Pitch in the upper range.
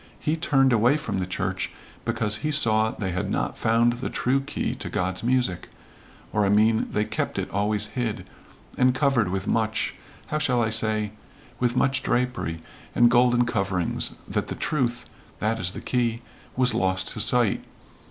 No: low, 115 Hz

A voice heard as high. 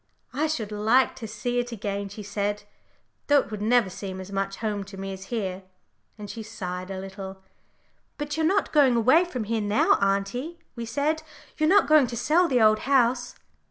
Yes: high, 220 Hz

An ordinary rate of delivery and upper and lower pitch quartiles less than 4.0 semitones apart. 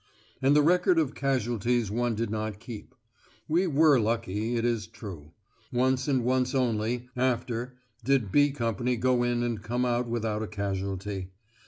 Yes: average, 160 wpm; average, 3.0 semitones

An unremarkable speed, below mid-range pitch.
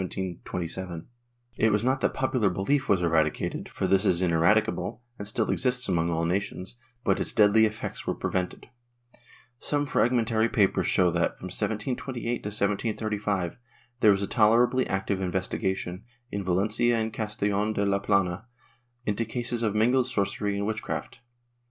Yes: average, 150 wpm; low, 105 Hz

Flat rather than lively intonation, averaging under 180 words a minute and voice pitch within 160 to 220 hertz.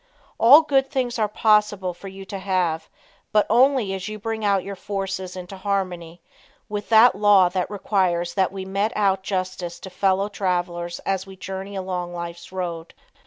Yes: narrow, 2.3 semitones; average, 165 wpm; high, 190 Hz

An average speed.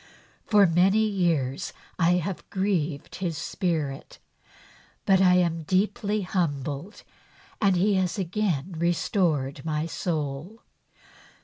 No: slow, 105 wpm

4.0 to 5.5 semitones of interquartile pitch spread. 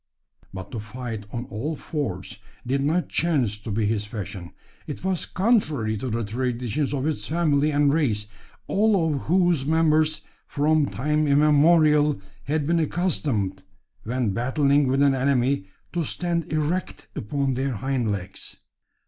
Yes: average, 5.0 semitones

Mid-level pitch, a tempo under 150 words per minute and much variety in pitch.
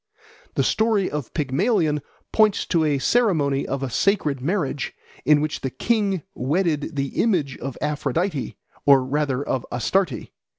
Yes: medium, 150 Hz; average, 140 wpm; wide, 5.7 semitones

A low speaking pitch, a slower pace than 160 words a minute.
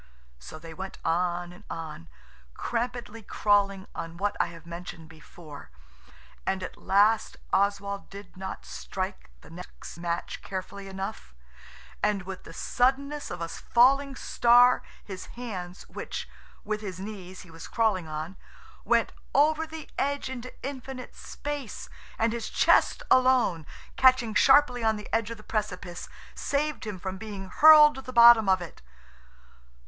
No: high, 205 Hz; average, 145 wpm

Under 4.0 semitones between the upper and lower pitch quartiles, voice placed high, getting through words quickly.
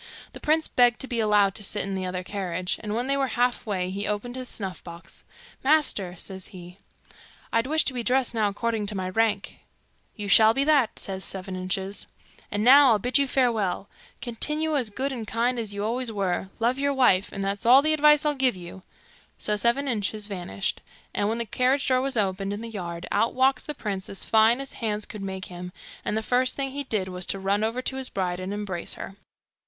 No: average, 4.7 semitones; high, 215 Hz; fast, 220 wpm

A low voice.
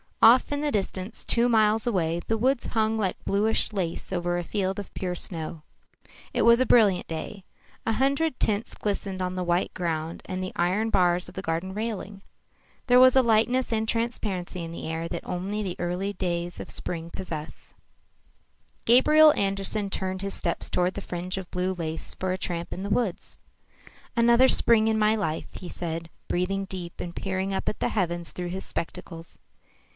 No: high, 190 Hz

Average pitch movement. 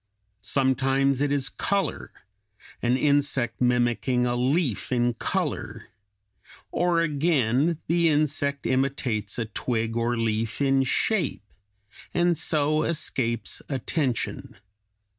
Yes: average, 3.8 semitones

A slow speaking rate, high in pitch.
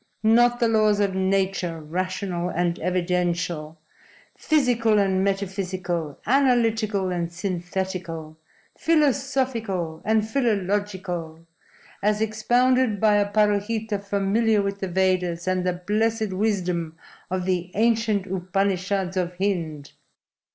Yes: slow, 105 wpm; high, 195 Hz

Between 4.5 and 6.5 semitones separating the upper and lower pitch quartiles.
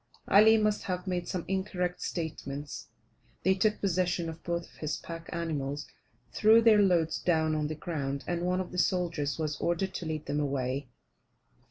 No: average, 3.4 semitones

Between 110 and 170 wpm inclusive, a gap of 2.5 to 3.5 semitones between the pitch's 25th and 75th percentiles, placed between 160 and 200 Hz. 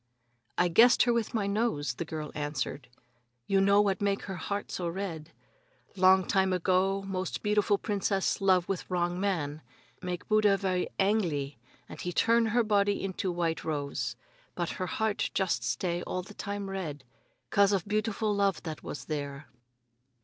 Yes: average, 160 wpm; average, 3.1 semitones; high, 190 Hz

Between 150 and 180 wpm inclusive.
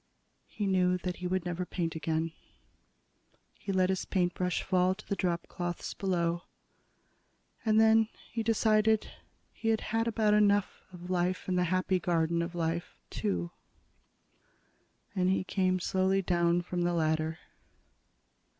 No: average, 140 wpm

